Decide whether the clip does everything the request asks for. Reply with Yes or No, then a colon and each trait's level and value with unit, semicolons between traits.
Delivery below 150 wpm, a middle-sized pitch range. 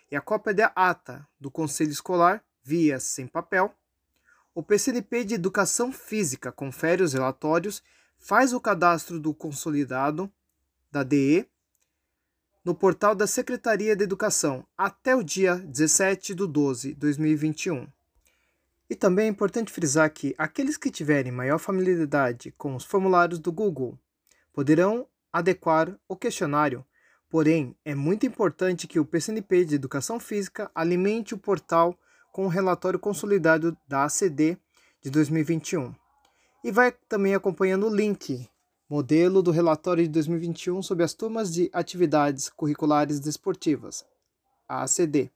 Yes: average, 135 wpm; average, 4.8 semitones